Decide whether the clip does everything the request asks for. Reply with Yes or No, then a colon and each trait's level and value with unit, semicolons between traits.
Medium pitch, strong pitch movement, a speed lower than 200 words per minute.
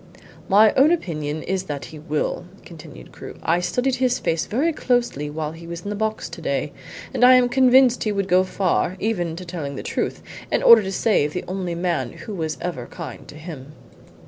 No: medium, 180 Hz; wide, 6.0 semitones; fast, 205 wpm